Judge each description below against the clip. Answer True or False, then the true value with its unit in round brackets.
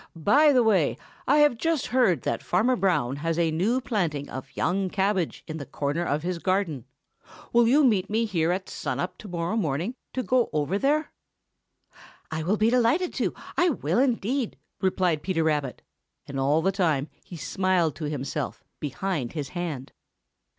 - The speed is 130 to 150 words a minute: False (175 wpm)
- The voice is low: False (185 Hz)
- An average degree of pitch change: False (6.6 semitones)